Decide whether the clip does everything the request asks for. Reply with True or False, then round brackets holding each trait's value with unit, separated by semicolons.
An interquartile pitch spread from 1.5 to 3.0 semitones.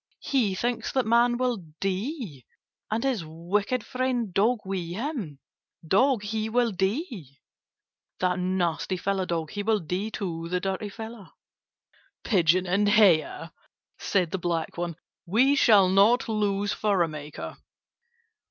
False (4.4 semitones)